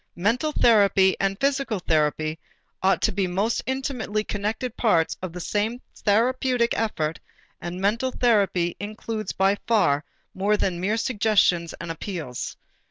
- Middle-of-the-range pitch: No, high, 205 Hz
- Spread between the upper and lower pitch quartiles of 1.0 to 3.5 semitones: No, average, 4.2 semitones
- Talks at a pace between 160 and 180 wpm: No, slow, 135 wpm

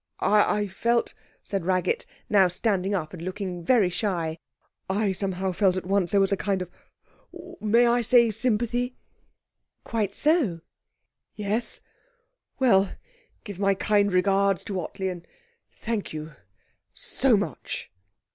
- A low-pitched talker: No, high, 200 Hz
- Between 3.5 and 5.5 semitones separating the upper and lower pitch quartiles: No, average, 2.9 semitones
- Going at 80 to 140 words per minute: Yes, slow, 135 wpm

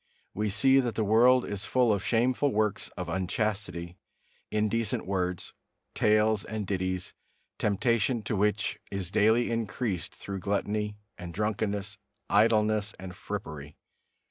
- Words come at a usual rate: No, slow, 125 wpm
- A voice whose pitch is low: Yes, low, 105 Hz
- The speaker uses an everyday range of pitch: No, narrow, 2.3 semitones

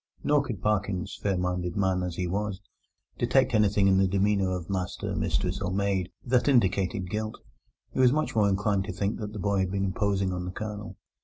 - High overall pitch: No, low, 100 Hz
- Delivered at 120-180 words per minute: No, fast, 205 wpm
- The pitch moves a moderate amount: No, narrow, 2.2 semitones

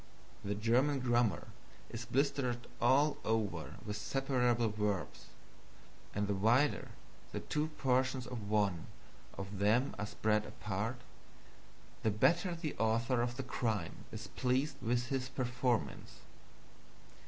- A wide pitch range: No, average, 3.5 semitones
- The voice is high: No, low, 120 Hz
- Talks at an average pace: No, slow, 120 wpm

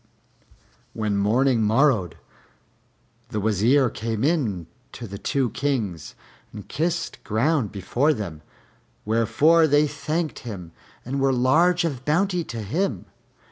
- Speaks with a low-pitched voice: Yes, low, 125 Hz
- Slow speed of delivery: Yes, slow, 120 wpm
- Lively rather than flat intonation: Yes, wide, 6.1 semitones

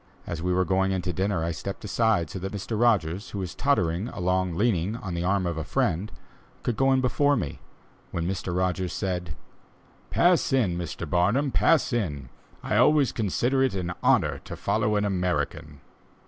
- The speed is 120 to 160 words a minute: No, average, 185 wpm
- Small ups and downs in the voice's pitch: No, average, 4.6 semitones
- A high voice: No, very low, 95 Hz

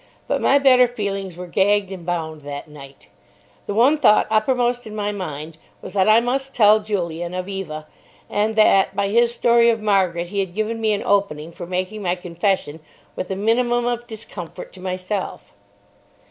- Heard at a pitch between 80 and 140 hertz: No, high, 200 Hz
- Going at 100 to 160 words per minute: No, average, 180 wpm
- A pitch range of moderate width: Yes, average, 4.1 semitones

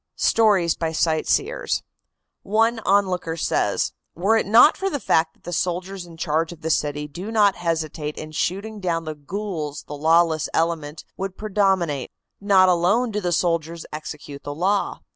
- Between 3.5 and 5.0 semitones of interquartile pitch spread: Yes, average, 4.1 semitones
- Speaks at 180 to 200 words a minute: No, average, 160 wpm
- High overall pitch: No, medium, 175 Hz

